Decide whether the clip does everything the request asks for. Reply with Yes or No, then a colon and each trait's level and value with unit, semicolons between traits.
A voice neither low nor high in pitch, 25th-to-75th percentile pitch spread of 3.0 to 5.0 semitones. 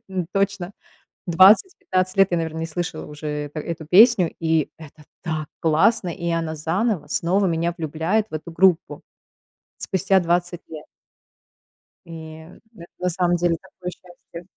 No: medium, 170 Hz; narrow, 2.6 semitones